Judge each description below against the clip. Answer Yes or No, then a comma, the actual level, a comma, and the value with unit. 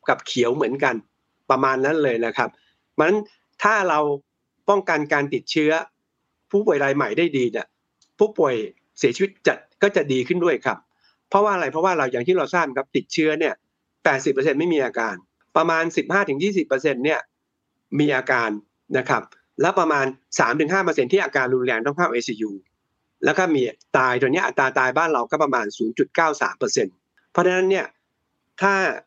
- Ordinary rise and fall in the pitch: No, wide, 6.4 semitones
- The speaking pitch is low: No, medium, 160 Hz